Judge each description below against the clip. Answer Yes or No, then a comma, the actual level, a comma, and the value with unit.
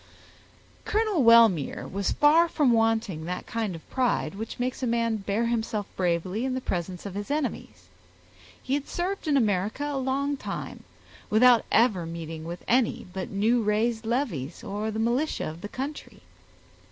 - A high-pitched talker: Yes, high, 225 Hz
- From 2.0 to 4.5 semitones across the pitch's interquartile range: No, average, 5.1 semitones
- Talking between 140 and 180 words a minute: Yes, average, 165 wpm